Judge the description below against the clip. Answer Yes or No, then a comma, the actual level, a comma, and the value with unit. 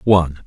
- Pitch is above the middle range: No, very low, 85 Hz